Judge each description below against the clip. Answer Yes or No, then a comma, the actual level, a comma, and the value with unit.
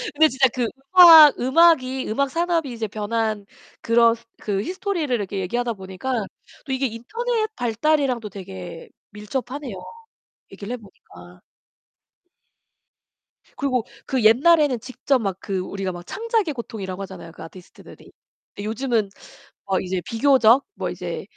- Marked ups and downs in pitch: Yes, wide, 5.7 semitones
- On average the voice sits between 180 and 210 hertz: No, high, 235 Hz